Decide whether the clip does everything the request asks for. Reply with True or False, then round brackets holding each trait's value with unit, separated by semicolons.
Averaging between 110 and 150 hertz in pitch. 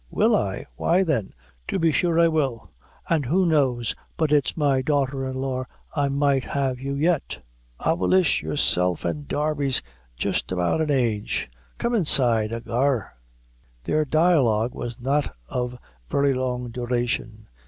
True (135 Hz)